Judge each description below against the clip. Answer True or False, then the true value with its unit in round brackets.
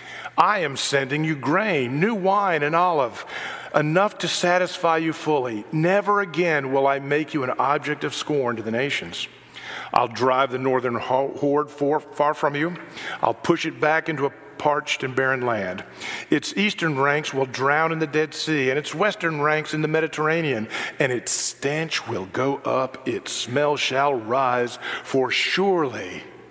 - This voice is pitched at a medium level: True (150 Hz)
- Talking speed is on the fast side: False (170 wpm)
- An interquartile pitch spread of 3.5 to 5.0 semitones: False (2.8 semitones)